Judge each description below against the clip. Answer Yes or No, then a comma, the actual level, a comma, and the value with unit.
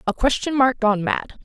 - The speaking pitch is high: Yes, high, 240 Hz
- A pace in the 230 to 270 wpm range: No, fast, 210 wpm